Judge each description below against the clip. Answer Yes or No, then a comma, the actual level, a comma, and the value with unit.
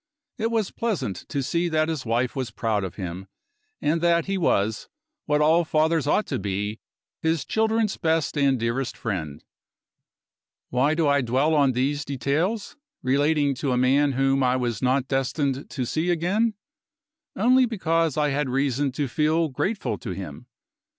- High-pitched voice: No, medium, 145 Hz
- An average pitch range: Yes, average, 4.4 semitones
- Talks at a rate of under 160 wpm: No, average, 165 wpm